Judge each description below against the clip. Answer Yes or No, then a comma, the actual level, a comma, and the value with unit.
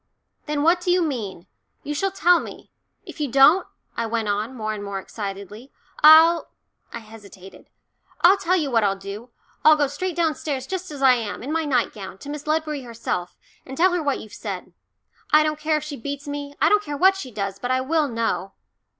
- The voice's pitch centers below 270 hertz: No, very high, 280 Hz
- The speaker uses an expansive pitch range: Yes, wide, 6.0 semitones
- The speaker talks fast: Yes, fast, 210 wpm